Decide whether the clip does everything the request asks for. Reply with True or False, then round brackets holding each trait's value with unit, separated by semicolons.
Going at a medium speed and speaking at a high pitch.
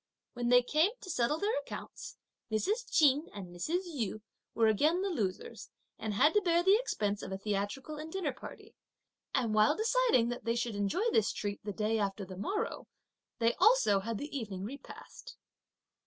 True (180 wpm; 245 Hz)